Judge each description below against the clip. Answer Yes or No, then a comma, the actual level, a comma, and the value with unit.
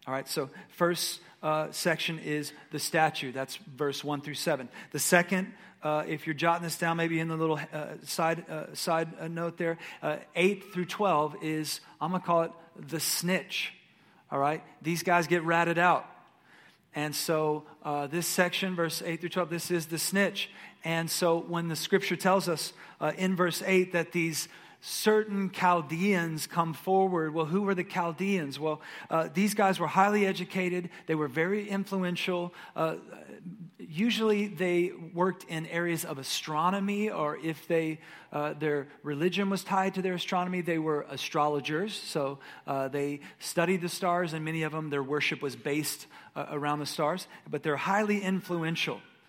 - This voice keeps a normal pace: Yes, average, 170 wpm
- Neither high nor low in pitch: Yes, medium, 170 Hz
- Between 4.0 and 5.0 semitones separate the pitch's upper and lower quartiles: No, average, 2.9 semitones